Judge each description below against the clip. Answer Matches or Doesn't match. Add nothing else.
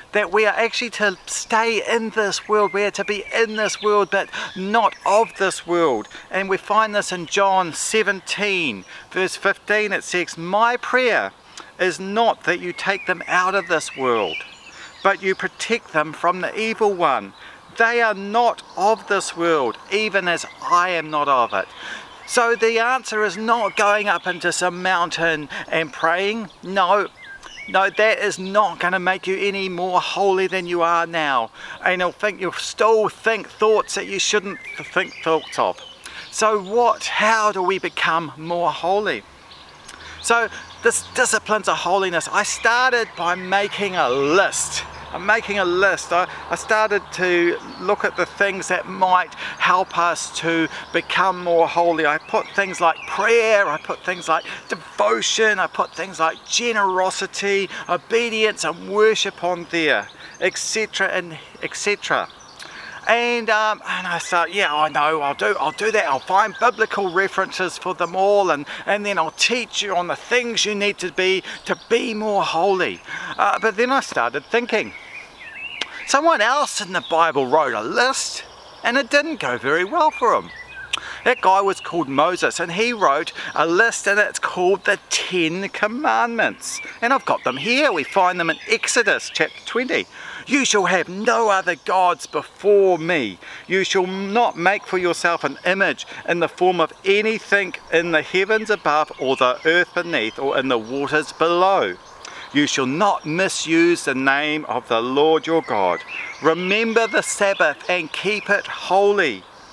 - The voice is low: Doesn't match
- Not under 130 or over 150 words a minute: Doesn't match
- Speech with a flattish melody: Doesn't match